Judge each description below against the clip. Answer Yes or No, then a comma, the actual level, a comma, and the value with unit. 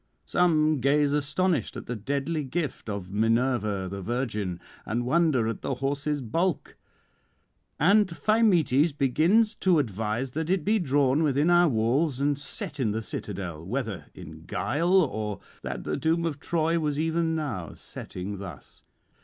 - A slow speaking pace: No, average, 150 wpm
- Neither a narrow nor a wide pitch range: No, wide, 6.7 semitones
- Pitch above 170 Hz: No, medium, 140 Hz